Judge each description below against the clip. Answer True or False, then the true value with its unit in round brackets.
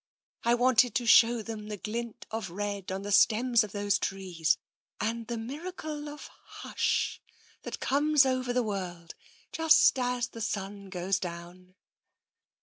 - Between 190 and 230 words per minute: False (155 wpm)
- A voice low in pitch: False (220 Hz)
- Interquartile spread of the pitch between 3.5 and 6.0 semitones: True (4.3 semitones)